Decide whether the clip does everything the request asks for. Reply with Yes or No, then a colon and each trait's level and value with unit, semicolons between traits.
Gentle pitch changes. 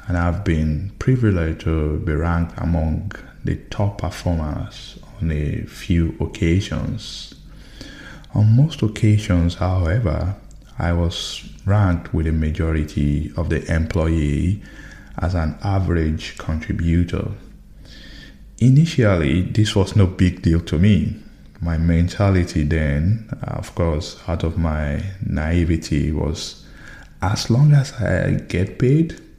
No: average, 4.3 semitones